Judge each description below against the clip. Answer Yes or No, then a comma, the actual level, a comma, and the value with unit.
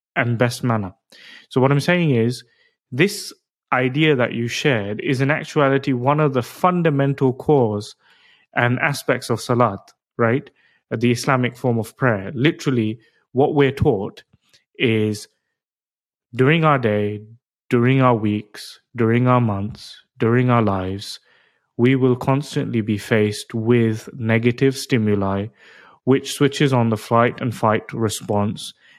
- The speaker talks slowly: Yes, slow, 130 wpm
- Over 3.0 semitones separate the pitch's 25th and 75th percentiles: Yes, average, 3.5 semitones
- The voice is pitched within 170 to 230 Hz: No, low, 125 Hz